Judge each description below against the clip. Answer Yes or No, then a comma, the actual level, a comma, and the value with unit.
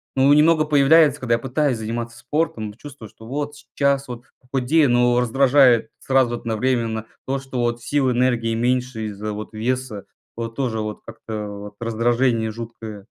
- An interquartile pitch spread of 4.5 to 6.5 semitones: No, average, 3.1 semitones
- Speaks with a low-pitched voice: Yes, low, 120 Hz